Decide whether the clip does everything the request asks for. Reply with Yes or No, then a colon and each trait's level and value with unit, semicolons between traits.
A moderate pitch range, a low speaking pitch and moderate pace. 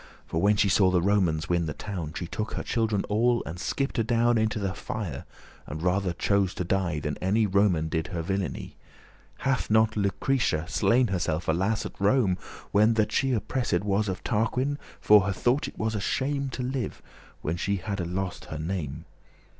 Yes: average, 4.0 semitones; low, 100 Hz; average, 190 wpm